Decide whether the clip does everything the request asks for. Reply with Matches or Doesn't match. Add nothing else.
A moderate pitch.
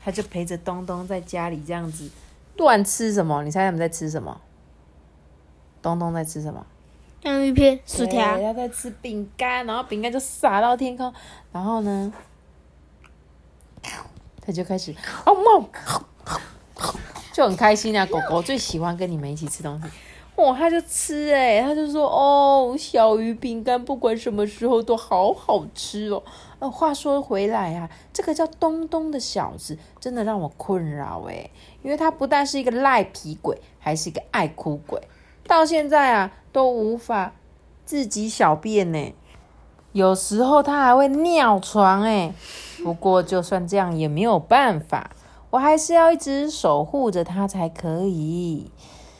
Doesn't match